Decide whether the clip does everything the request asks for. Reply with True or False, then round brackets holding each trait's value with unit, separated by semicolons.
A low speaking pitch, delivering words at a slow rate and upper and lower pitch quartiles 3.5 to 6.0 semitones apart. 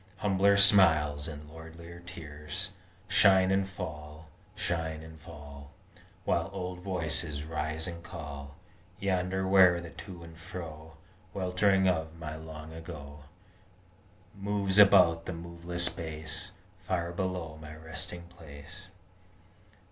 False (85 Hz; 115 wpm; 3.0 semitones)